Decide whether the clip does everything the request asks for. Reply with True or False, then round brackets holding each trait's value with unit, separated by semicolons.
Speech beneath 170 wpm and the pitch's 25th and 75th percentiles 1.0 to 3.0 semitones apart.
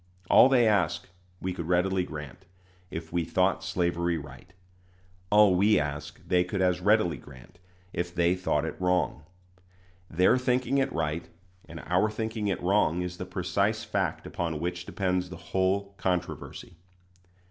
True (150 wpm; 2.4 semitones)